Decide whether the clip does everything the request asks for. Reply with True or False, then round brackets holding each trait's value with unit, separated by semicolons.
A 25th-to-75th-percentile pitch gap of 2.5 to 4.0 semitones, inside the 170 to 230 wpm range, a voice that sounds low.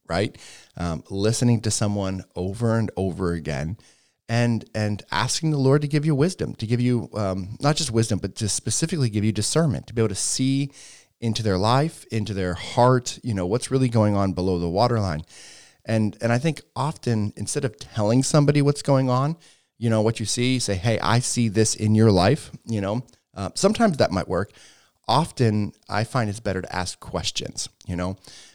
False (4.5 semitones; 200 wpm; 115 Hz)